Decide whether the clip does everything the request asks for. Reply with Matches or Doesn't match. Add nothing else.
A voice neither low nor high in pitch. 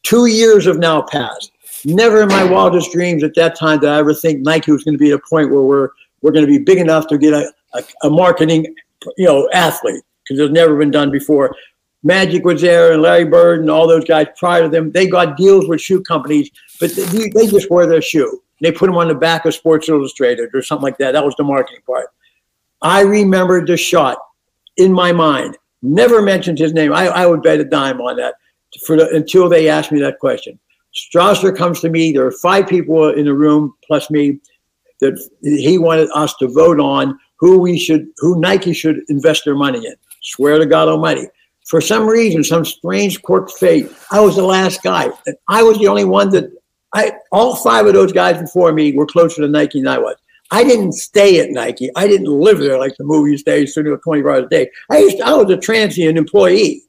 Matches